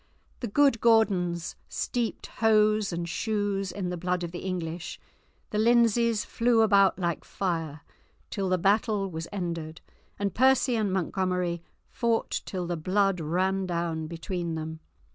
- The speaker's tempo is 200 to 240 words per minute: No, average, 145 wpm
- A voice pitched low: No, high, 190 Hz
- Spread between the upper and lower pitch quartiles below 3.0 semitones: No, average, 3.8 semitones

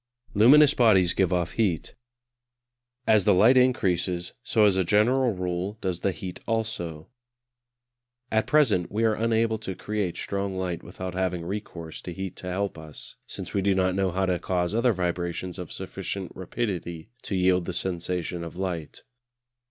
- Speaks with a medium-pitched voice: No, very low, 95 Hz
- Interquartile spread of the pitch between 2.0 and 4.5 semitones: Yes, average, 3.2 semitones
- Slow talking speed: No, average, 165 wpm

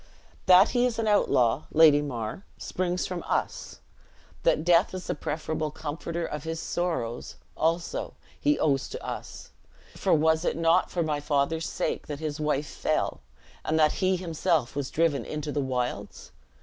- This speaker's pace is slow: No, average, 160 wpm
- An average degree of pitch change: Yes, average, 3.0 semitones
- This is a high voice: No, medium, 160 Hz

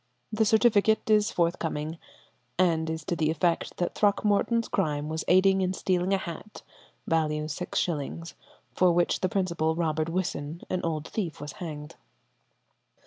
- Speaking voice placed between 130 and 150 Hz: No, medium, 170 Hz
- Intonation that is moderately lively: Yes, average, 3.2 semitones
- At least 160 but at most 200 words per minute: No, average, 140 wpm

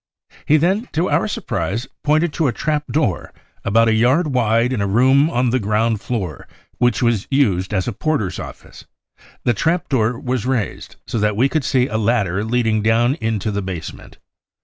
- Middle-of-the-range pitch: No, low, 120 Hz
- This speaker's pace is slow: No, average, 185 wpm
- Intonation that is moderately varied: Yes, average, 4.1 semitones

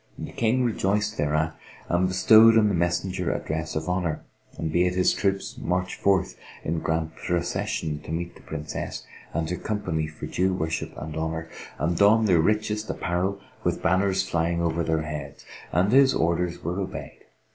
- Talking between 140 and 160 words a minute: No, average, 170 wpm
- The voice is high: No, very low, 90 Hz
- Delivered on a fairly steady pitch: No, average, 3.5 semitones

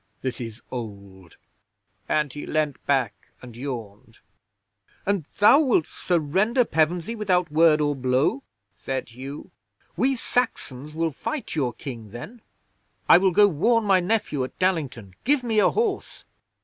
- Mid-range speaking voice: Yes, medium, 155 Hz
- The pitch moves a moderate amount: No, wide, 8.1 semitones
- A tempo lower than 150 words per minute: Yes, average, 140 wpm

